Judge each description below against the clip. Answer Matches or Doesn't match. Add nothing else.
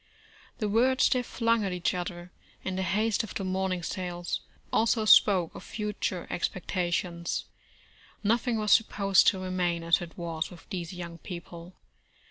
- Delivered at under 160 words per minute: Matches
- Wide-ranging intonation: Doesn't match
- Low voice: Doesn't match